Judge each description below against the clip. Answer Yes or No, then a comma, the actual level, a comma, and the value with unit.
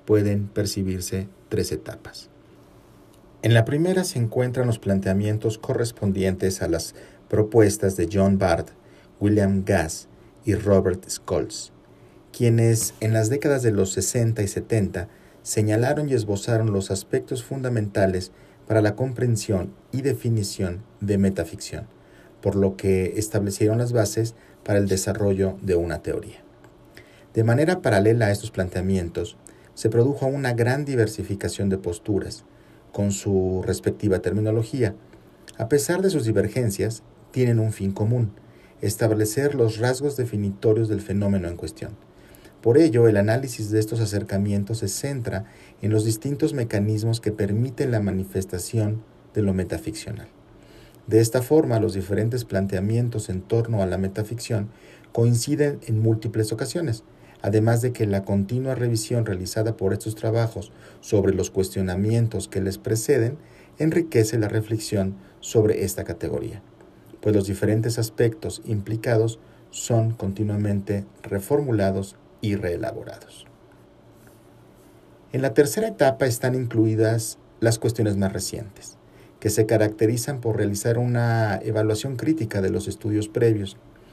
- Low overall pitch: Yes, low, 110 Hz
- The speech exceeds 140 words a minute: No, average, 130 wpm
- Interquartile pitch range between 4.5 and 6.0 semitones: No, average, 2.9 semitones